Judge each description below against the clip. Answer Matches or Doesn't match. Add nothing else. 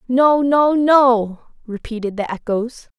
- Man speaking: Doesn't match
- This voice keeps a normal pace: Doesn't match